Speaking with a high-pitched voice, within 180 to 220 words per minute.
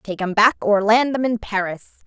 No: high, 215 Hz; fast, 230 wpm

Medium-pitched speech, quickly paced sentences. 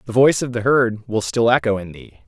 No: low, 115 Hz; fast, 265 wpm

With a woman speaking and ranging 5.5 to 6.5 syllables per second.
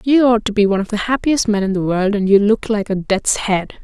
Yes: female; 5.7 syllables/s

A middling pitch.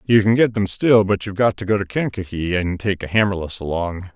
No: low, 100 Hz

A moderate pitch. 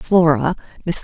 Yes: medium, 165 Hz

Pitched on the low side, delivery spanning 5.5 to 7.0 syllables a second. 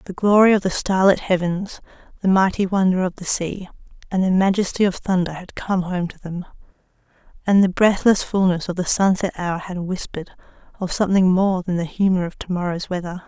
No: medium, 185 Hz; 5.6 syllables/s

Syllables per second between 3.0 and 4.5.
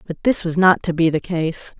No: 5.2 syllables/s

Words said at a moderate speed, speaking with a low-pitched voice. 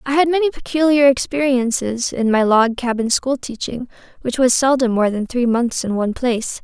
No: average, 190 wpm; very high, 250 Hz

